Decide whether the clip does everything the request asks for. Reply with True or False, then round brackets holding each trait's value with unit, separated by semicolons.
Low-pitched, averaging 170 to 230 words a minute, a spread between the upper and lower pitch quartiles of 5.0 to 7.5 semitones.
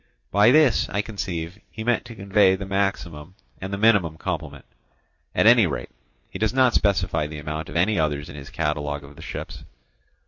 True (95 Hz; 185 wpm; 5.3 semitones)